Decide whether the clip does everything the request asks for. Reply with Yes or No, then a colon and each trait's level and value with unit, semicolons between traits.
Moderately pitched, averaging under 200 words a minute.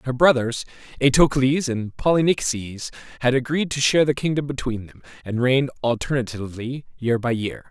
No: low, 130 Hz; average, 150 wpm